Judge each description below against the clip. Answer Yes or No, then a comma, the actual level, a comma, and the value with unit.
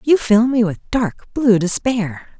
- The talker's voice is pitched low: No, high, 220 Hz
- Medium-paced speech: Yes, average, 175 wpm